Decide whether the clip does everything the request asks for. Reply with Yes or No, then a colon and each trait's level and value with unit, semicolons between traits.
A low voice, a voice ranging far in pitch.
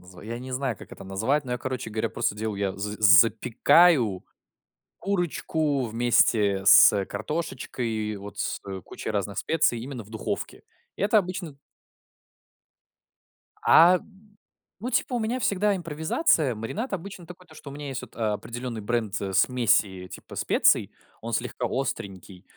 Yes: low, 120 Hz; wide, 7.0 semitones